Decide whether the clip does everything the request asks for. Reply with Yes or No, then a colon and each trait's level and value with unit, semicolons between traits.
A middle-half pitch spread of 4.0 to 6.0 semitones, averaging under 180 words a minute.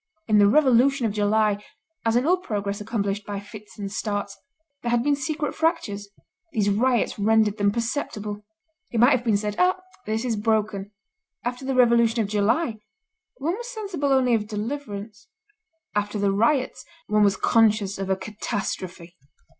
No: average, 3.6 semitones; average, 160 wpm